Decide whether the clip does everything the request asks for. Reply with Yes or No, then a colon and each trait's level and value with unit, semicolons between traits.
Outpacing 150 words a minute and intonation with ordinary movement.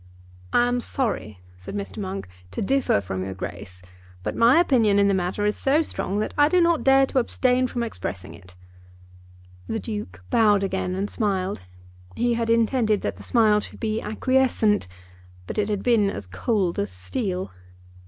Yes: average, 175 wpm; average, 4.7 semitones